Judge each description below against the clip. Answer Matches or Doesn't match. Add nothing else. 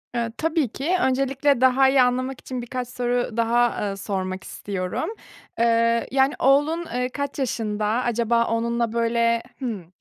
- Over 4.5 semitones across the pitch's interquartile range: Doesn't match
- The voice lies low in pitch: Doesn't match